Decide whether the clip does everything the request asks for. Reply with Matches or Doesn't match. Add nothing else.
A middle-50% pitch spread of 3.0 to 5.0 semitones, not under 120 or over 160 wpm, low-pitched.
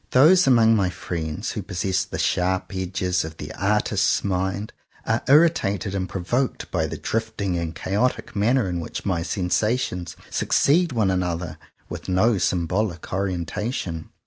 Matches